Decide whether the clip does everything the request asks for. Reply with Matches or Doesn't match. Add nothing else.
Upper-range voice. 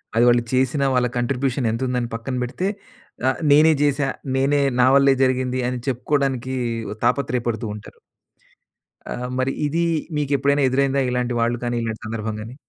Doesn't match